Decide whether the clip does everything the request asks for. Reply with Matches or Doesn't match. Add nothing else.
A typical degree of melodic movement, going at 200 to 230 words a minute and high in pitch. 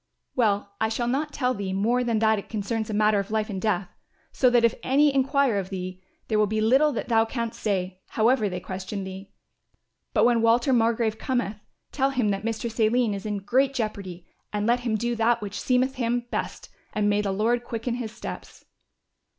Matches